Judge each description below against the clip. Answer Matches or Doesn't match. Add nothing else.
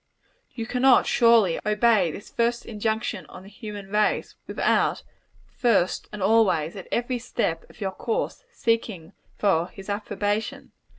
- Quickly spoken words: Doesn't match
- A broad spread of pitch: Doesn't match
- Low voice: Doesn't match